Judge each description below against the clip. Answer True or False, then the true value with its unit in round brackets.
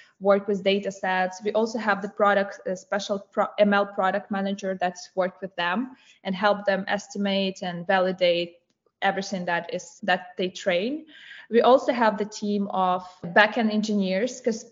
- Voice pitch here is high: True (200 Hz)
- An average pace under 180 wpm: True (165 wpm)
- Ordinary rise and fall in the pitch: False (2.3 semitones)